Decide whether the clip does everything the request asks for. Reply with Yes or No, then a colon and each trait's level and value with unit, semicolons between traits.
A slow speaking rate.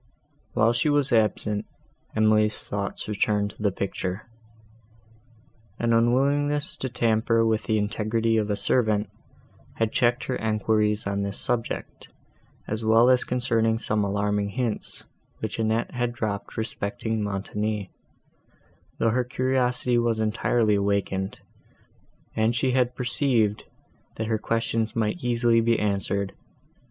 Yes: slow, 125 wpm